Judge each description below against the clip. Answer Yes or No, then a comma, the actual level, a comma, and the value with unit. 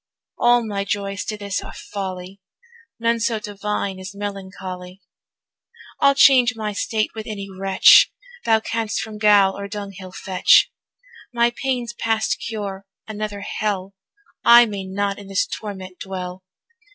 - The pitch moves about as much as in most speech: No, narrow, 2.3 semitones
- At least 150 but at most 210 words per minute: No, average, 140 wpm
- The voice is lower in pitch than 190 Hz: No, high, 205 Hz